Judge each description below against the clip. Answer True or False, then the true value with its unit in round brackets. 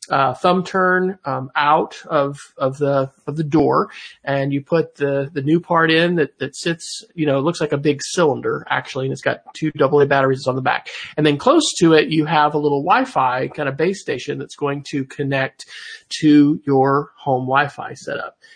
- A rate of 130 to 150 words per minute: False (200 wpm)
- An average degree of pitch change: True (3.1 semitones)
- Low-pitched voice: False (145 Hz)